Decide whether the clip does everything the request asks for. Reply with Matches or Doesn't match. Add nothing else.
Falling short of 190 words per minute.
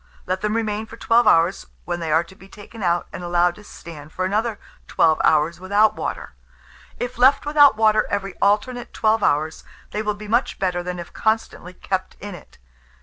Doesn't match